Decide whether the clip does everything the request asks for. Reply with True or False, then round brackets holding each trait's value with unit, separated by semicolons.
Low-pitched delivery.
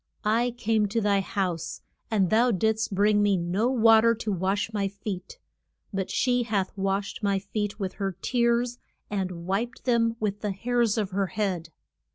False (205 Hz)